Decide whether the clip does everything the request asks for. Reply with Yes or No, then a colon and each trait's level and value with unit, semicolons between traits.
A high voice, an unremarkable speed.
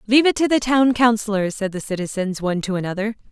No: high, 215 Hz; fast, 215 wpm